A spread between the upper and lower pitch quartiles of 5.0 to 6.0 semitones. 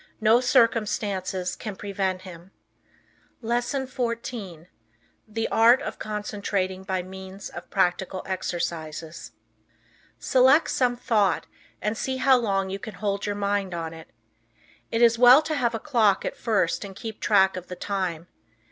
No: average, 3.8 semitones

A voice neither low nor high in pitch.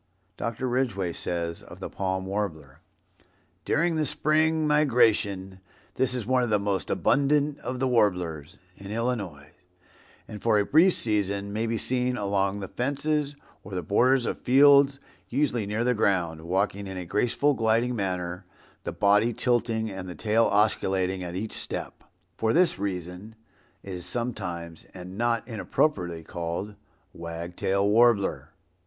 No: low, 105 Hz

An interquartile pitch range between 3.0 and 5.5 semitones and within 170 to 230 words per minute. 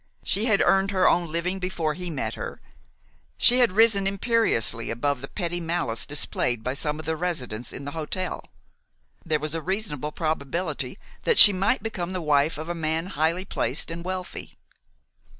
Yes: average, 4.0 semitones; average, 175 wpm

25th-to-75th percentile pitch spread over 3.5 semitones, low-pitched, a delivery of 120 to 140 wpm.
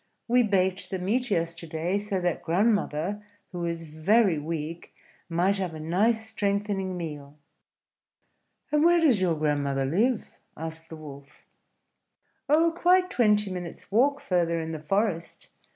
No: average, 4.6 semitones; medium, 185 Hz; slow, 135 wpm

